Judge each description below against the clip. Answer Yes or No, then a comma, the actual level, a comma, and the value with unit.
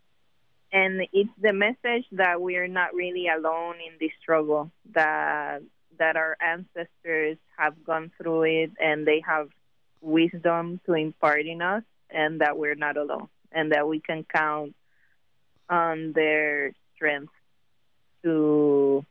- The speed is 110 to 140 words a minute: Yes, slow, 135 wpm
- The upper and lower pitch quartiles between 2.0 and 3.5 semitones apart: Yes, narrow, 2.4 semitones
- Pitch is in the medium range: Yes, medium, 160 Hz